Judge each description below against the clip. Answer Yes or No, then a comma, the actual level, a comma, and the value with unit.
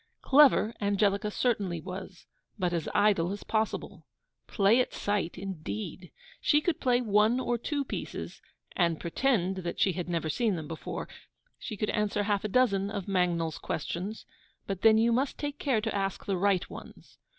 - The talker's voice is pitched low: No, high, 200 Hz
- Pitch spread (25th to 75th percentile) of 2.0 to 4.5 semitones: Yes, average, 3.9 semitones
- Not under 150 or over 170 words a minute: Yes, average, 165 wpm